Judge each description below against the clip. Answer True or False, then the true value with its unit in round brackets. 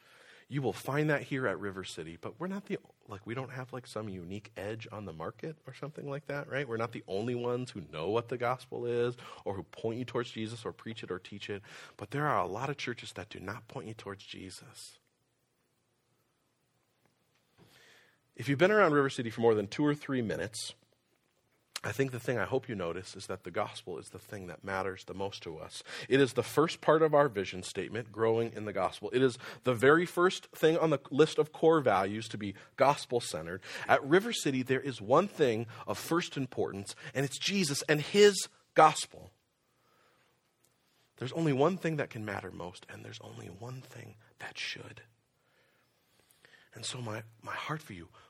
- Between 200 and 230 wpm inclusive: True (205 wpm)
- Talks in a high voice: False (120 Hz)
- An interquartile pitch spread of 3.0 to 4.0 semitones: False (4.8 semitones)